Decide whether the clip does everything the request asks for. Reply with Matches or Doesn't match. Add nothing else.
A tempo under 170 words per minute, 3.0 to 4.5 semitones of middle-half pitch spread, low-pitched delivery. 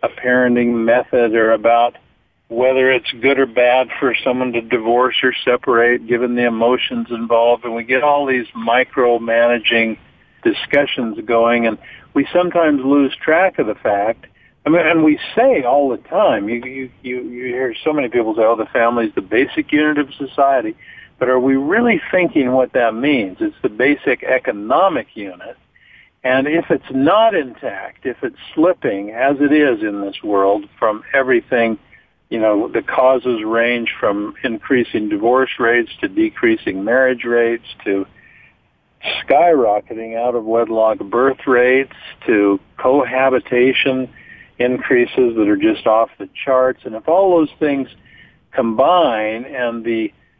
Matches